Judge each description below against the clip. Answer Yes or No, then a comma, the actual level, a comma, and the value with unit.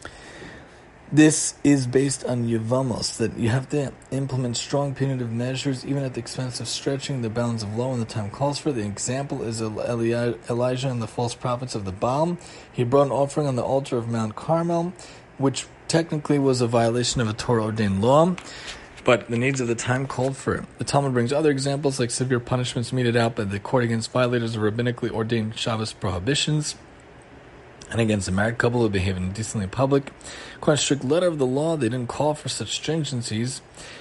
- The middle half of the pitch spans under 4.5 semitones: Yes, average, 3.2 semitones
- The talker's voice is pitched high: No, low, 125 Hz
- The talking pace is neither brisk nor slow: Yes, average, 190 wpm